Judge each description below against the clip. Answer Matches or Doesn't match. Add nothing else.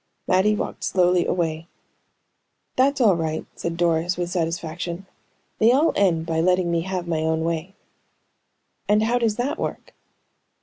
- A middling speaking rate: Matches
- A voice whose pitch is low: Doesn't match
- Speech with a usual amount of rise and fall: Matches